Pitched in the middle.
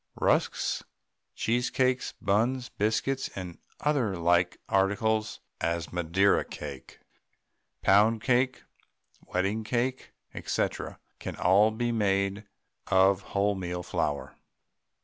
No: low, 100 Hz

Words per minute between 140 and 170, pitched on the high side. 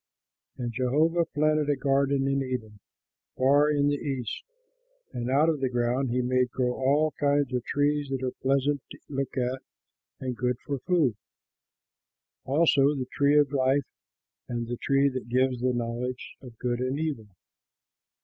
No: average, 160 wpm; low, 135 Hz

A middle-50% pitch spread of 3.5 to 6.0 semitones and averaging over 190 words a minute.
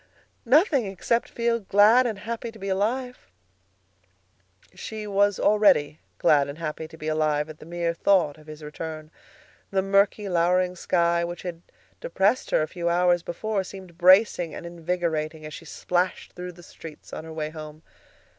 No: average, 4.2 semitones; average, 165 wpm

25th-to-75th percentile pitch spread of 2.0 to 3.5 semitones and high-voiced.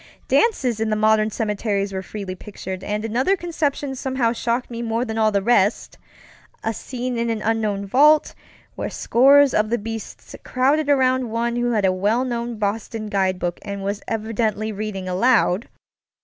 Yes: average, 3.1 semitones; high, 225 Hz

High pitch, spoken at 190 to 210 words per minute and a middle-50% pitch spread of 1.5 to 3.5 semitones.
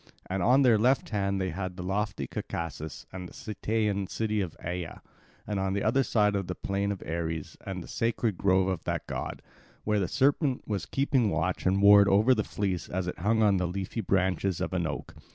No: low, 100 Hz; fast, 205 wpm; average, 2.8 semitones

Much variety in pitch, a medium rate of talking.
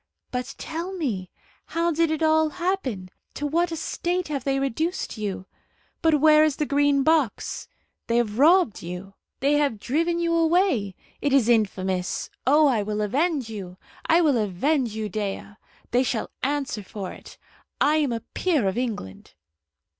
Yes: wide, 6.9 semitones; average, 165 wpm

